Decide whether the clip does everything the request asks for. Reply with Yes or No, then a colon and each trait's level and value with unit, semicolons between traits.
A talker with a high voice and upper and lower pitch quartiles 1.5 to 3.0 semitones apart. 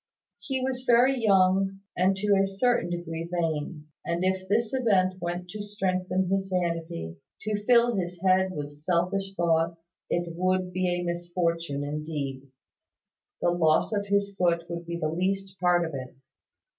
No: medium, 180 Hz; narrow, 2.5 semitones